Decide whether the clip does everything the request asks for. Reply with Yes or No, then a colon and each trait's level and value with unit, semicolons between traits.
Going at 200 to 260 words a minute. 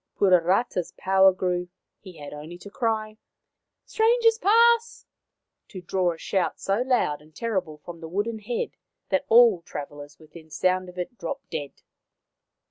No: average, 160 wpm